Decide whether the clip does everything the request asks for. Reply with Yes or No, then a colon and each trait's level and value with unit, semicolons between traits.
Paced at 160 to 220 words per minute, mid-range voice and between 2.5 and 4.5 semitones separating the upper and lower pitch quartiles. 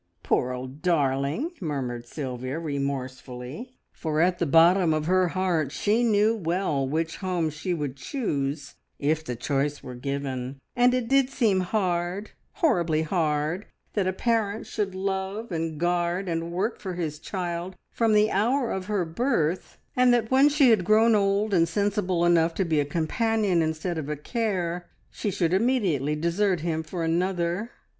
No: average, 165 wpm; medium, 175 Hz; average, 5.0 semitones